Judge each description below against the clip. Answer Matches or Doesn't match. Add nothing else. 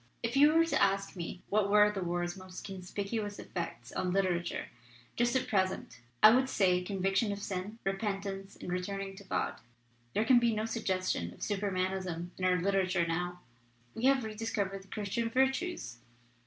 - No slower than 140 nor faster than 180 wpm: Matches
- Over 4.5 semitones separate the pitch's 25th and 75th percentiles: Doesn't match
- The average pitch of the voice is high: Matches